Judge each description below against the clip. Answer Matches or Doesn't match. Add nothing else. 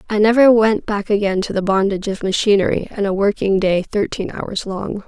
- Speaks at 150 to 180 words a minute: Doesn't match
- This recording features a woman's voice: Matches